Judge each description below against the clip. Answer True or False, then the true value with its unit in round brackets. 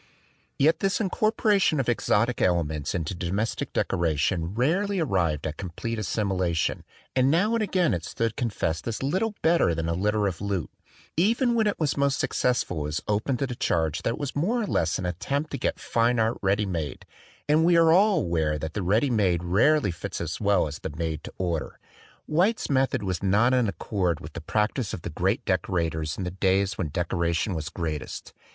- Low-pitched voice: True (100 Hz)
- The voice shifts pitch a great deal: True (8.7 semitones)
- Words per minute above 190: True (200 wpm)